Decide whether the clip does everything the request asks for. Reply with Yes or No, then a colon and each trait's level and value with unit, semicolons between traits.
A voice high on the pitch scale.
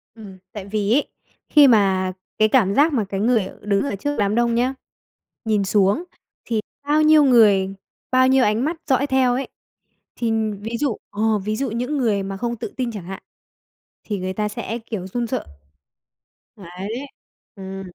Yes: high, 220 Hz